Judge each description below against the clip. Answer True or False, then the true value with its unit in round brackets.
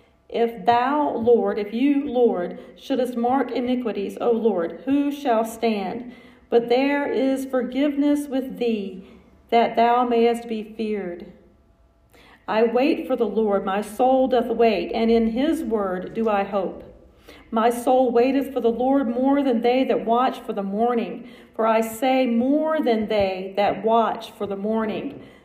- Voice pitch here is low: False (235 Hz)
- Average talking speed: True (155 wpm)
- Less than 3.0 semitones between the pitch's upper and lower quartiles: True (2.6 semitones)